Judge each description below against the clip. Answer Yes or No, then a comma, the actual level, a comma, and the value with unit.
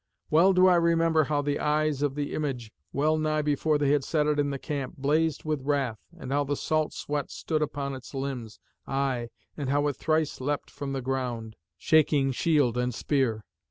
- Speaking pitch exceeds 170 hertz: No, medium, 145 Hz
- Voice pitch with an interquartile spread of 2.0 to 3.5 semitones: Yes, narrow, 2.5 semitones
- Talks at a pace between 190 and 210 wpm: Yes, average, 195 wpm